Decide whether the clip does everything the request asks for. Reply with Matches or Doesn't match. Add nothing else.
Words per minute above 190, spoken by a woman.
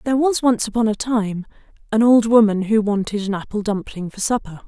Matches